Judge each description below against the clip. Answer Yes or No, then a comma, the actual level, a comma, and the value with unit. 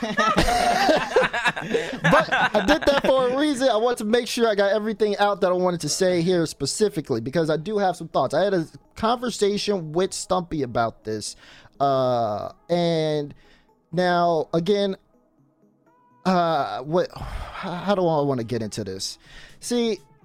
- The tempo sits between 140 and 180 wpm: Yes, average, 155 wpm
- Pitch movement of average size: No, wide, 6.3 semitones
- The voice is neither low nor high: Yes, medium, 180 Hz